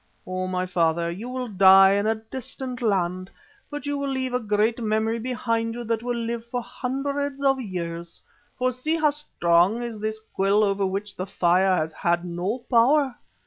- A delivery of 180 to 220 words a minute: Yes, average, 185 wpm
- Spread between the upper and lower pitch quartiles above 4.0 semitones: Yes, average, 5.2 semitones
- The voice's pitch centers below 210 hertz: No, high, 220 Hz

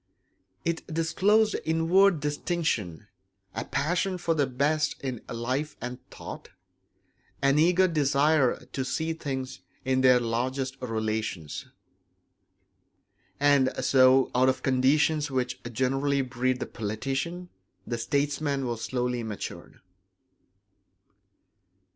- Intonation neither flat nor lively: Yes, average, 3.7 semitones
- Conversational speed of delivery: No, slow, 105 wpm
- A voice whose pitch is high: No, low, 135 Hz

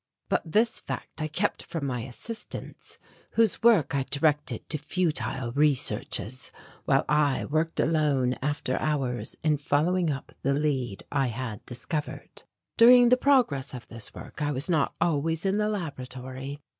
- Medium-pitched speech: Yes, medium, 145 Hz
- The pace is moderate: Yes, average, 150 wpm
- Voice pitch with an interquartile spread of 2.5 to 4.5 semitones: Yes, average, 4.0 semitones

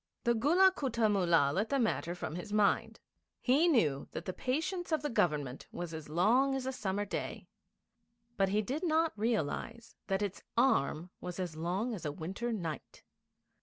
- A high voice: Yes, high, 210 Hz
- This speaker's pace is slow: No, average, 175 wpm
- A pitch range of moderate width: No, wide, 6.7 semitones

